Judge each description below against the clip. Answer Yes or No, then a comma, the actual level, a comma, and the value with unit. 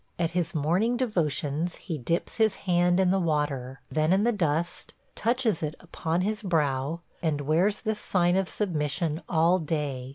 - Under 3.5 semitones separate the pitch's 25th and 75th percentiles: No, average, 3.9 semitones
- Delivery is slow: No, average, 165 wpm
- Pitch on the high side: No, medium, 170 Hz